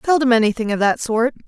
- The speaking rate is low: No, fast, 205 wpm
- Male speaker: No, female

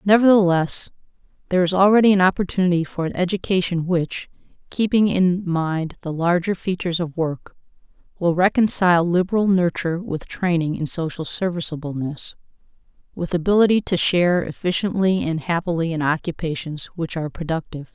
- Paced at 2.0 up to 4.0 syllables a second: No, 5.6 syllables/s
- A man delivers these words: No, female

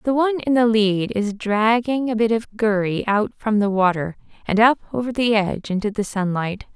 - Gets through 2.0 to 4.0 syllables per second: No, 5.0 syllables/s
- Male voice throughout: No, female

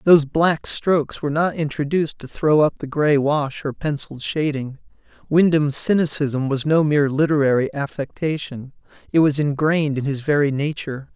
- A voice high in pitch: No, medium, 145 Hz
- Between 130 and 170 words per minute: Yes, average, 155 wpm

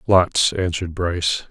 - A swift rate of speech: No, slow, 120 wpm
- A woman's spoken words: No, male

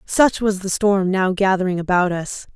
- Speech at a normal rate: Yes, average, 190 wpm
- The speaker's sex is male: No, female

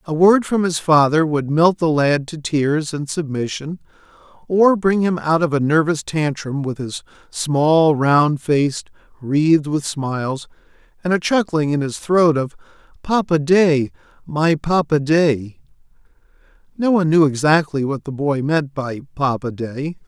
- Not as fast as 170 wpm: Yes, average, 155 wpm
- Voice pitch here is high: No, medium, 155 Hz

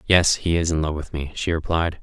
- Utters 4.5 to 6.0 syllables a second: Yes, 5.5 syllables/s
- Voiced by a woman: No, male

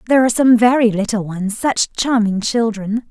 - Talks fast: No, average, 155 wpm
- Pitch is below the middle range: No, high, 225 Hz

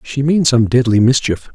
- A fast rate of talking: No, average, 195 wpm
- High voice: No, low, 125 Hz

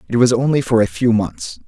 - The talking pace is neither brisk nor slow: No, fast, 250 wpm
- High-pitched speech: No, low, 115 Hz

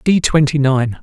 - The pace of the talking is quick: No, average, 175 wpm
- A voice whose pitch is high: No, medium, 140 Hz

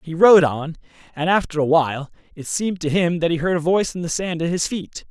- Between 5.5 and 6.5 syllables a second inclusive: Yes, 6.0 syllables/s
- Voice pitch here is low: No, medium, 170 Hz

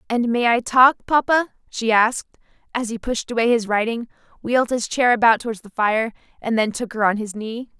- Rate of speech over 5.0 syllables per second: Yes, 5.5 syllables/s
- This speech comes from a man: No, female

